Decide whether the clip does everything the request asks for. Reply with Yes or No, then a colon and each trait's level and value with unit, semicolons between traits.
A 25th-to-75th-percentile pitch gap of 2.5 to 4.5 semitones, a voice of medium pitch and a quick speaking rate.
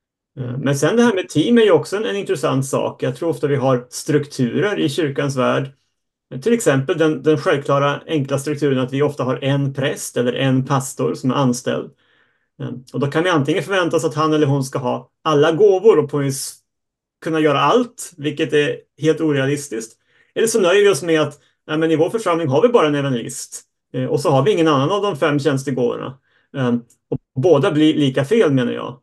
Yes: average, 3.1 semitones; medium, 145 Hz; fast, 200 wpm